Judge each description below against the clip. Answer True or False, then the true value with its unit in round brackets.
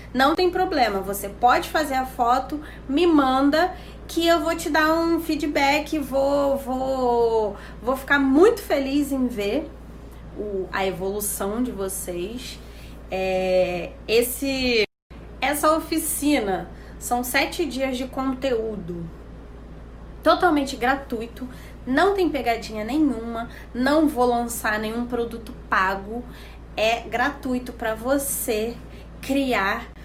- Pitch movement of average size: True (4.6 semitones)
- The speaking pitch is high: True (255 Hz)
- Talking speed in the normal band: False (110 wpm)